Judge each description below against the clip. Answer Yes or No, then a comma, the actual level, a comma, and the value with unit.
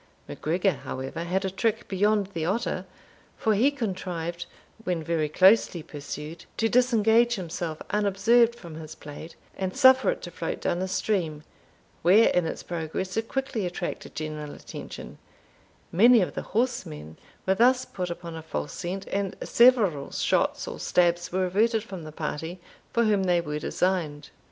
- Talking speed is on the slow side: No, average, 160 wpm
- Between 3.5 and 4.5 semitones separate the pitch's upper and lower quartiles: No, average, 5.0 semitones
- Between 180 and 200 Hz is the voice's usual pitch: Yes, medium, 185 Hz